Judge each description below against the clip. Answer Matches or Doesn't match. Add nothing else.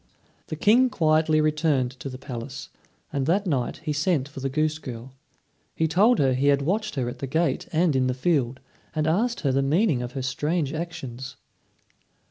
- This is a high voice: Doesn't match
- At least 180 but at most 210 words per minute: Matches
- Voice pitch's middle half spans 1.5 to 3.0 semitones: Doesn't match